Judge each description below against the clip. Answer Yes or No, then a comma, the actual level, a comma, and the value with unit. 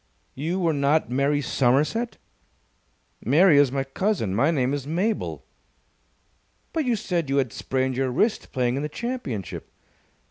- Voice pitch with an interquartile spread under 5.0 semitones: No, wide, 5.4 semitones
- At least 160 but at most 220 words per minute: No, average, 145 wpm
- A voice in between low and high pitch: Yes, medium, 145 Hz